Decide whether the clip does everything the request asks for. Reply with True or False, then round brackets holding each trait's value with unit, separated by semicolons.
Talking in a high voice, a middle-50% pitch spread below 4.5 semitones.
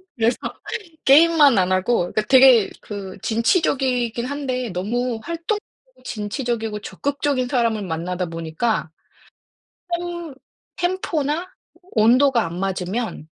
False (235 Hz; 5.5 semitones)